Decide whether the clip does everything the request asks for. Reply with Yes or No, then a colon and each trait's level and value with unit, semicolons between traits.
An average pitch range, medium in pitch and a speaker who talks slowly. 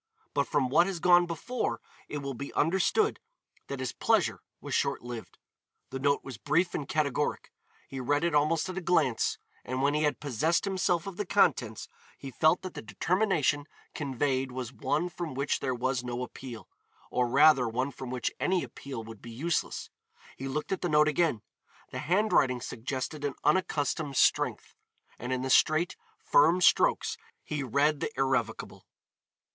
No: average, 4.4 semitones; medium, 145 Hz; average, 170 wpm